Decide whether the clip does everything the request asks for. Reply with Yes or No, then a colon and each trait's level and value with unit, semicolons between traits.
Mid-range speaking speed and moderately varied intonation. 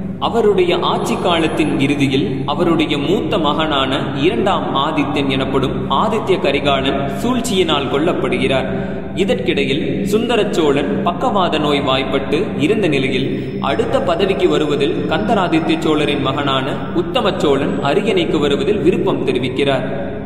Yes: average, 95 wpm; average, 4.6 semitones